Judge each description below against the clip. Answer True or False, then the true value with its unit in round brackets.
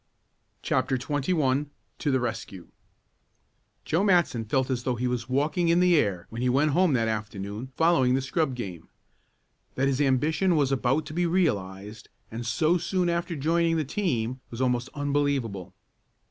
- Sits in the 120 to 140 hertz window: True (135 Hz)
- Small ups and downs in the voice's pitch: False (5.2 semitones)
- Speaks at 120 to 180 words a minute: True (160 wpm)